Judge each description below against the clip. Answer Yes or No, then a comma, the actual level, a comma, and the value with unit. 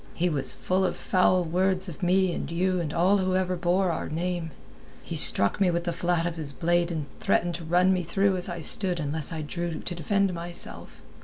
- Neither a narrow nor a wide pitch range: No, narrow, 1.8 semitones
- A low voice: No, medium, 175 Hz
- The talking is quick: Yes, fast, 215 wpm